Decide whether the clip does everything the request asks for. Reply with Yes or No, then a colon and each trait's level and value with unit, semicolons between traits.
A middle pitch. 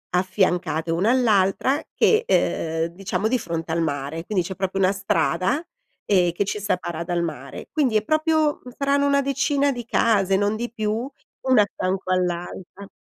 No: high, 195 Hz